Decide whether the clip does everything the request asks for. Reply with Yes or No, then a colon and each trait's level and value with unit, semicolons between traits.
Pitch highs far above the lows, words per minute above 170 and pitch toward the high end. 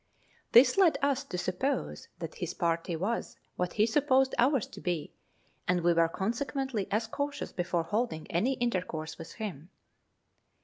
No: wide, 7.2 semitones; average, 150 wpm; high, 210 Hz